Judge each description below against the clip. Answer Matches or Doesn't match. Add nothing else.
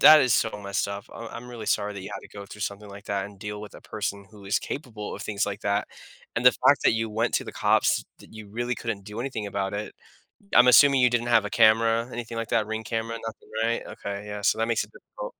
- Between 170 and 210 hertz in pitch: Doesn't match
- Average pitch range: Doesn't match